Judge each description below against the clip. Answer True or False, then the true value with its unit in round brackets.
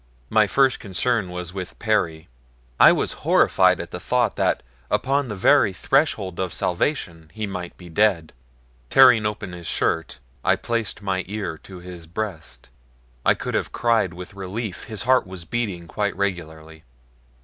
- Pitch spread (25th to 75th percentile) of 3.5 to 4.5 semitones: True (3.9 semitones)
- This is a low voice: True (95 Hz)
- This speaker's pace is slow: False (160 wpm)